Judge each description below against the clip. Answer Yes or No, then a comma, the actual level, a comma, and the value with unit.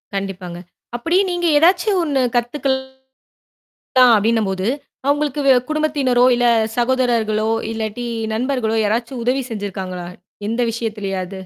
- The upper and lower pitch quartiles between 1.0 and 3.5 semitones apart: No, average, 4.2 semitones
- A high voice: Yes, high, 240 Hz